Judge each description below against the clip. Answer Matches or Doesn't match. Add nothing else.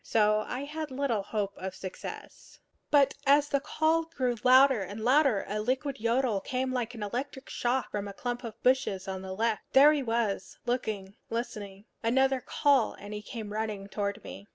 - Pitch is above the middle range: Matches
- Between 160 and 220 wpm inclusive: Matches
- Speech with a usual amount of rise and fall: Matches